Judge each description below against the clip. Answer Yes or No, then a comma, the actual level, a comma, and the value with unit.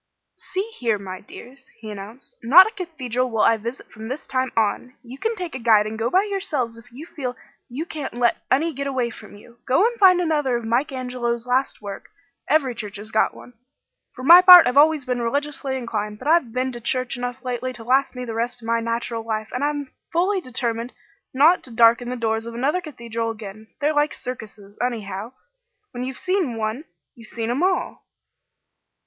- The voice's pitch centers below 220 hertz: No, very high, 250 Hz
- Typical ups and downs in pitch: Yes, average, 3.9 semitones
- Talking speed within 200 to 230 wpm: Yes, fast, 205 wpm